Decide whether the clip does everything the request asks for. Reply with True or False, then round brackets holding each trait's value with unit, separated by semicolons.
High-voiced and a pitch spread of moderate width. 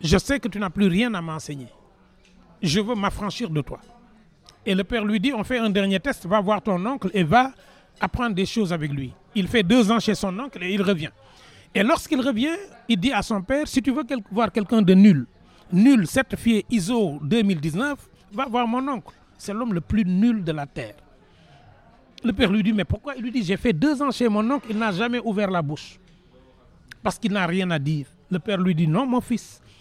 True (210 Hz; 4.4 semitones)